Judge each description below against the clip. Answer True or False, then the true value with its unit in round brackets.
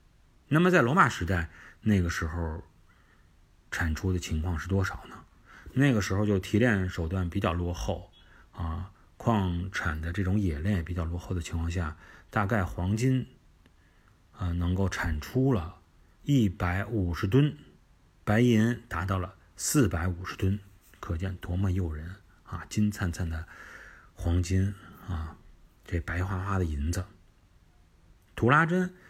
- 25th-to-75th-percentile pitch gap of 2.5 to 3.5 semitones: True (3.1 semitones)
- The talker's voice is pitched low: True (90 Hz)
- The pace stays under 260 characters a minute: True (205 characters per minute)